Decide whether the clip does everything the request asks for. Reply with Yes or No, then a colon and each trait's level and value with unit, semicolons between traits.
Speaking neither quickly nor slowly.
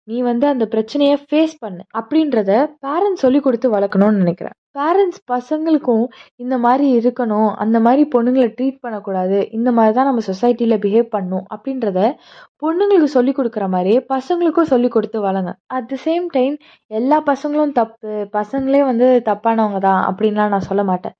No: fast, 150 wpm